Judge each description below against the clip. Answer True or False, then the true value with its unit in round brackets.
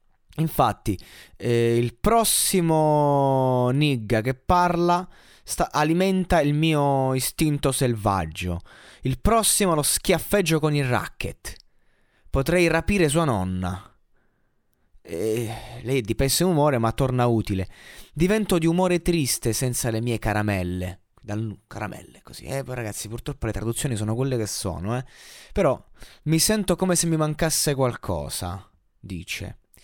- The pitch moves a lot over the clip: True (6.7 semitones)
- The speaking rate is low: False (125 wpm)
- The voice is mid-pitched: False (130 Hz)